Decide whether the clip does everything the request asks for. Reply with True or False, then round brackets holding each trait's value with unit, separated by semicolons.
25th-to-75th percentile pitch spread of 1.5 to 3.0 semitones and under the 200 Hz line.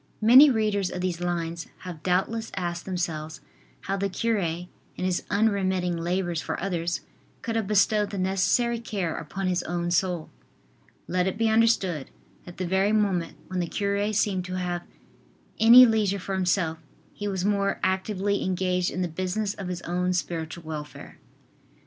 True (2.5 semitones; 185 Hz)